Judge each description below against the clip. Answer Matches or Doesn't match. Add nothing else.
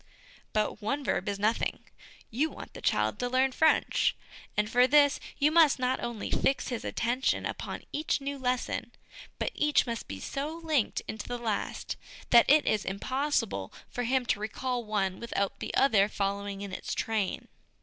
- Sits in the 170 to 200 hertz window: Doesn't match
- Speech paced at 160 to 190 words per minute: Matches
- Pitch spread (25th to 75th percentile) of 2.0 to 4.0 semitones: Doesn't match